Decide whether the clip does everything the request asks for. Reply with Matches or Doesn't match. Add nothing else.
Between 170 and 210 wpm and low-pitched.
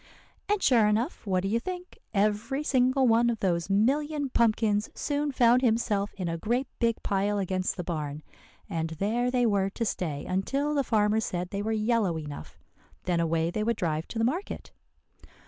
Doesn't match